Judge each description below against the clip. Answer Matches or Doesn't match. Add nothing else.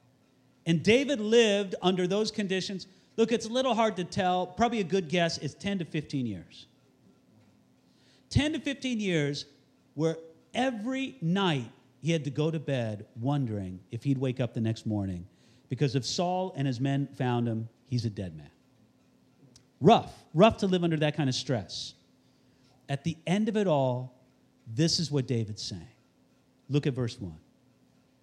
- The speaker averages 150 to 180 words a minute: Matches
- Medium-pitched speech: Matches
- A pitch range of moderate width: Doesn't match